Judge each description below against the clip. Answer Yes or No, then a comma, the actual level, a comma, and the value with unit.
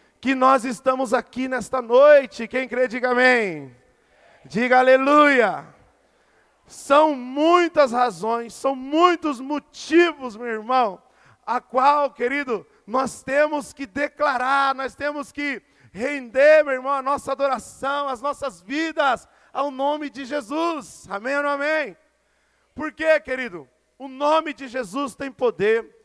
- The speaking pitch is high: Yes, very high, 275 Hz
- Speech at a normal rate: Yes, average, 130 wpm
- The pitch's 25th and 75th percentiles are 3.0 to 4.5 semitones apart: No, narrow, 2.4 semitones